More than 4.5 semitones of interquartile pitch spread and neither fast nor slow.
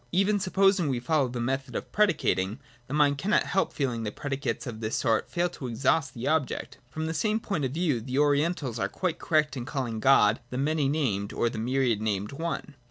No: average, 5.0 semitones; fast, 210 wpm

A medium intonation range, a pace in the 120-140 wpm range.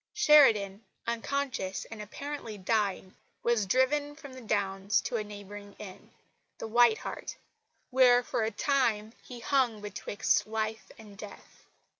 Yes: average, 3.8 semitones; slow, 135 wpm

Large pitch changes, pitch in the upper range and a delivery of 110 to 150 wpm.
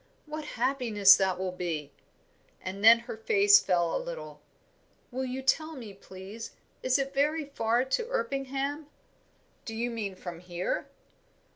Yes: wide, 6.6 semitones; high, 240 Hz; average, 145 wpm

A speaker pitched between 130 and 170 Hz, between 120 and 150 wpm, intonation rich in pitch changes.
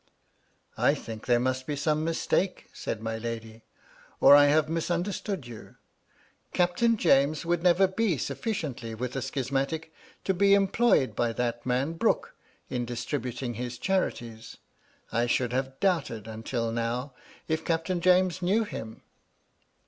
Yes: medium, 140 Hz; average, 140 wpm; wide, 6.6 semitones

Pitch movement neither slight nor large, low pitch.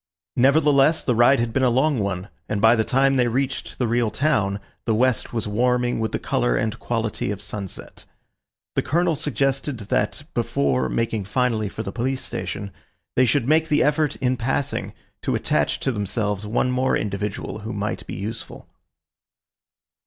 Yes: average, 4.2 semitones; low, 120 Hz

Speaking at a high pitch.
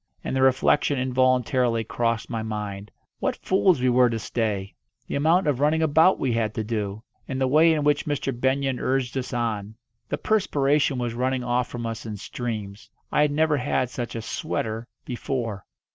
No: low, 125 Hz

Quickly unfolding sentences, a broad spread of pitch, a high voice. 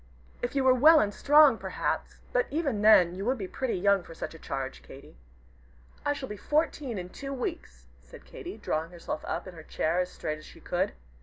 Yes: fast, 215 wpm; wide, 8.4 semitones; high, 205 Hz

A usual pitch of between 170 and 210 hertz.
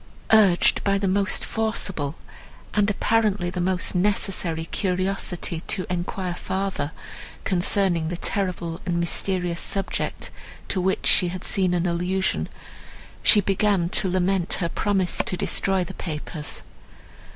Yes: medium, 185 Hz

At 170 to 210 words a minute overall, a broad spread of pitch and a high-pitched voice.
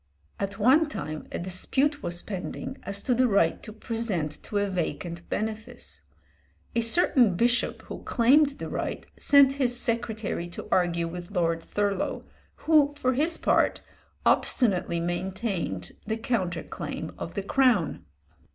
No: average, 145 wpm; wide, 6.2 semitones; high, 210 Hz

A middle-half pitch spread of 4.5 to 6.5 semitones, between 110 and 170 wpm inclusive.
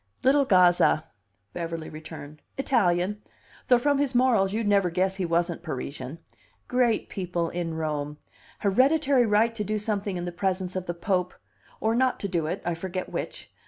Yes: average, 4.8 semitones; average, 165 wpm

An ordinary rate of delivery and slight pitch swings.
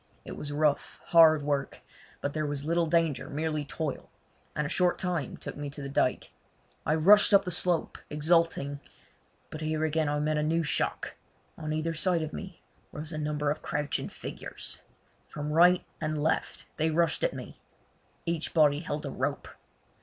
Yes: average, 175 wpm; narrow, 2.1 semitones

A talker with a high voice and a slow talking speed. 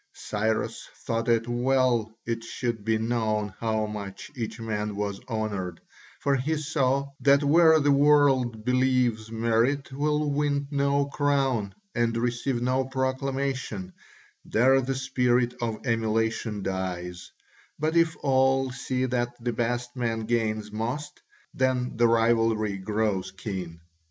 No: low, 120 Hz; slow, 130 wpm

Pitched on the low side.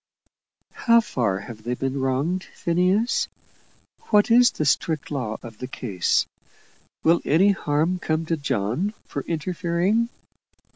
No: medium, 160 Hz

